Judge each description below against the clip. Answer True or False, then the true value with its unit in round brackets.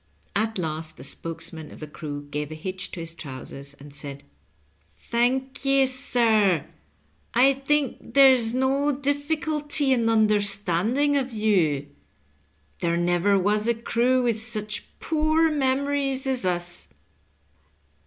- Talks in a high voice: True (225 Hz)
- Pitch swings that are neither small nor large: False (7.9 semitones)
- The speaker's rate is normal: False (130 wpm)